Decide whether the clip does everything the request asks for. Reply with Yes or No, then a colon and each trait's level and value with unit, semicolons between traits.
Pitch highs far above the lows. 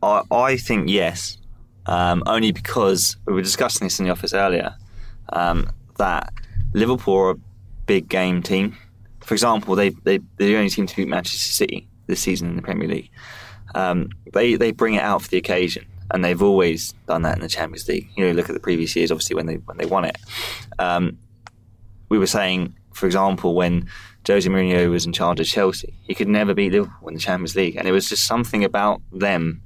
No: narrow, 2.5 semitones